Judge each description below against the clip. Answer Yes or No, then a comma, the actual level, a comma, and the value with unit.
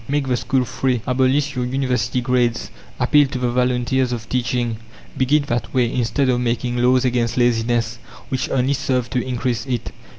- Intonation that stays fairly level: Yes, narrow, 1.4 semitones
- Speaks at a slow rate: No, average, 170 wpm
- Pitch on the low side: Yes, low, 125 Hz